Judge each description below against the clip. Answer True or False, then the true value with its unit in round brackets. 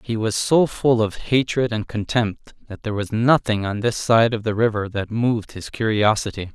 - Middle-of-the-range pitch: False (110 Hz)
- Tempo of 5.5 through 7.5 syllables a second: False (4.9 syllables/s)